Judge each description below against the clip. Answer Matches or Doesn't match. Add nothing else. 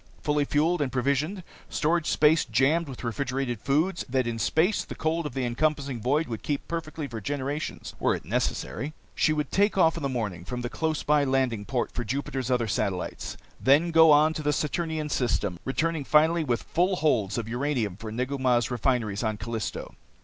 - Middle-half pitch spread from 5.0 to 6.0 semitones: Doesn't match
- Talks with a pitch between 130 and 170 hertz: Matches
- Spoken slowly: Doesn't match